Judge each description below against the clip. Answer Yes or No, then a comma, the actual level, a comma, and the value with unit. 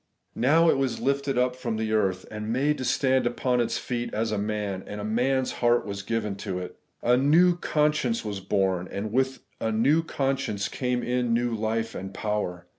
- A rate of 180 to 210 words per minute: Yes, average, 200 wpm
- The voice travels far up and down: No, average, 3.8 semitones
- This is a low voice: Yes, low, 115 Hz